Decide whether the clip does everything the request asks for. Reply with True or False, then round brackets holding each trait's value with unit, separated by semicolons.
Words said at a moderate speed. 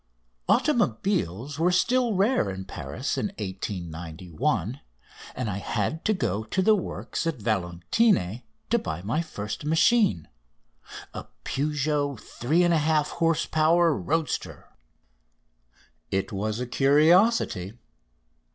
False (115 wpm)